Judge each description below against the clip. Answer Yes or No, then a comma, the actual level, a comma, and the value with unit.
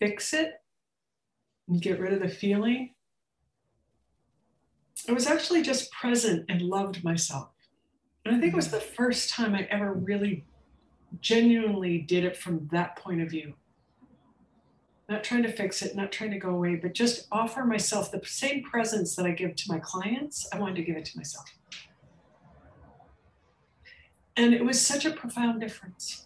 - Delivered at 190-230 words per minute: No, average, 165 wpm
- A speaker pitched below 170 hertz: No, high, 205 Hz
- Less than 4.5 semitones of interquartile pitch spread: No, average, 4.8 semitones